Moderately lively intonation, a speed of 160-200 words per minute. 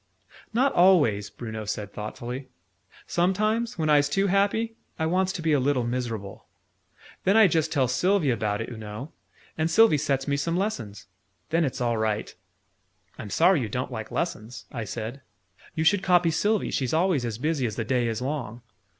No: wide, 7.3 semitones; average, 180 wpm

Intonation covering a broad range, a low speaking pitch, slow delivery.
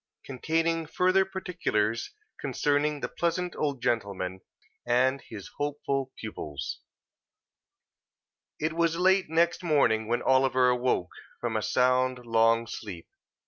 Yes: wide, 6.0 semitones; low, 130 Hz; slow, 110 wpm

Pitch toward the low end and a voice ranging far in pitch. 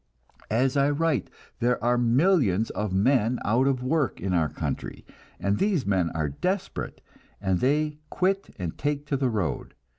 Yes: low, 125 Hz; wide, 6.5 semitones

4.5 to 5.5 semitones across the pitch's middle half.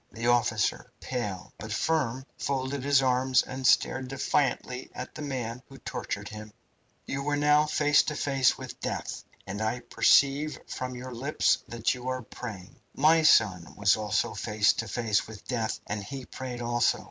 No: average, 3.6 semitones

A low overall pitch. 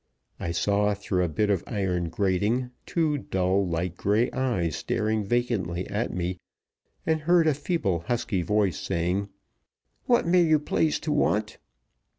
Yes: low, 105 Hz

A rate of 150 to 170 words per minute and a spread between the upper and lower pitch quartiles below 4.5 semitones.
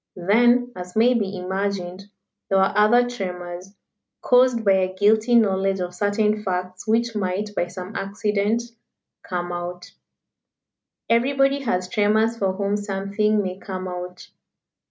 No: slow, 135 wpm; average, 3.1 semitones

